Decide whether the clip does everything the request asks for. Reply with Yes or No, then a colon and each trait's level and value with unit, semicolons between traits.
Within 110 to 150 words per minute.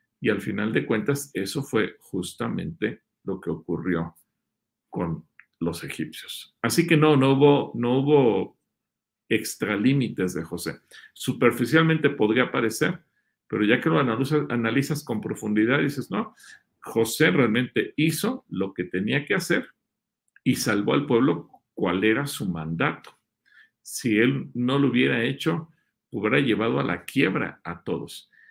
Yes: average, 140 wpm